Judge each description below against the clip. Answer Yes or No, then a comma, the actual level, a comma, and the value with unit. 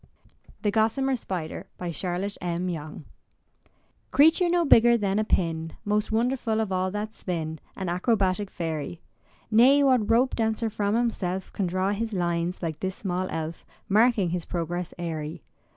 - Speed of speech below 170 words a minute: Yes, average, 150 wpm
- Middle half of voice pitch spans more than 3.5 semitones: Yes, average, 4.4 semitones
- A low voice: No, high, 195 Hz